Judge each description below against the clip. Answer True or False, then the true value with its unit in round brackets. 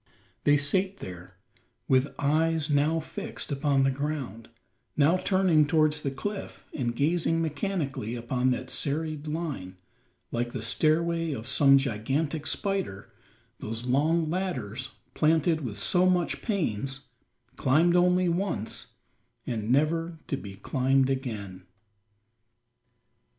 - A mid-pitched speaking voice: True (145 Hz)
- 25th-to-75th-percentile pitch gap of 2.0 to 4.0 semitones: False (4.4 semitones)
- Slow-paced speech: True (120 wpm)